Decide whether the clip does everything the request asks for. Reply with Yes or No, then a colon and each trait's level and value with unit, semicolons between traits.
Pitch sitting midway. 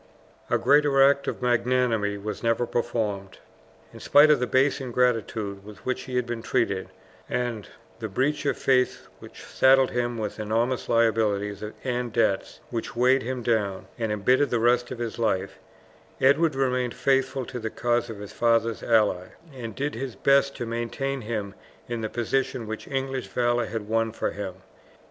No: low, 120 Hz